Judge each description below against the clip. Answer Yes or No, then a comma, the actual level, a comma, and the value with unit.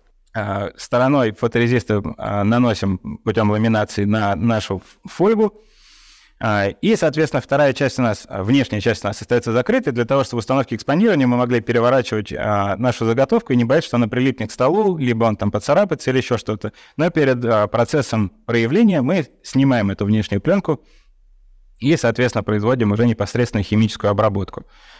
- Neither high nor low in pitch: No, low, 120 Hz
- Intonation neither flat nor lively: Yes, average, 4.0 semitones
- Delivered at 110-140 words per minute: No, average, 155 wpm